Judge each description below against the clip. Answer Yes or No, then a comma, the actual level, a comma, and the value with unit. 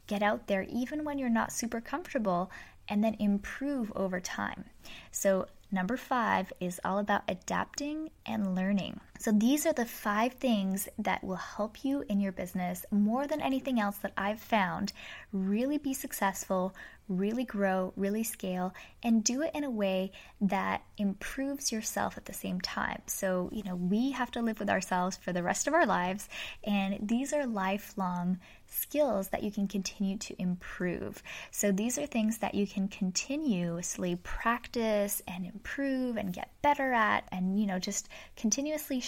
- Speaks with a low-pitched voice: No, high, 205 Hz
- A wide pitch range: No, average, 4.5 semitones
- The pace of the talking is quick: No, average, 165 wpm